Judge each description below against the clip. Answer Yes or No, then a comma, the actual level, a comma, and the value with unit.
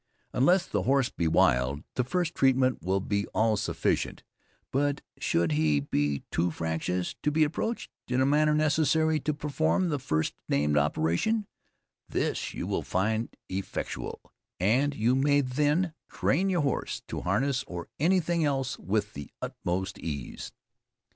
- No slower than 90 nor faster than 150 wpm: Yes, average, 145 wpm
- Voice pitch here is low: Yes, low, 125 Hz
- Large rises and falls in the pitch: Yes, wide, 9.0 semitones